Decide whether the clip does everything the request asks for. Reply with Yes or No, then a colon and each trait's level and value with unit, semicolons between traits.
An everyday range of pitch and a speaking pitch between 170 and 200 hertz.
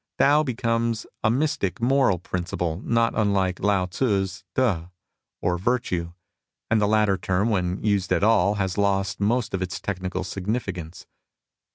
No: average, 3.9 semitones; low, 100 Hz